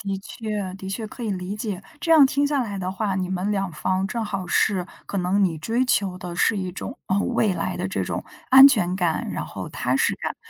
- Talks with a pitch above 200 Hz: No, high, 195 Hz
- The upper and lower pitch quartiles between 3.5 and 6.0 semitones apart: No, average, 3.1 semitones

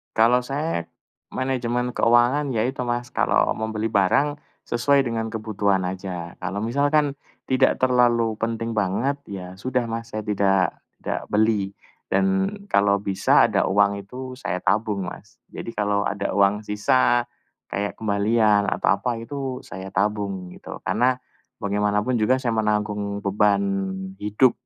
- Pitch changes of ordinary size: Yes, average, 3.4 semitones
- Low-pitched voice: Yes, low, 110 Hz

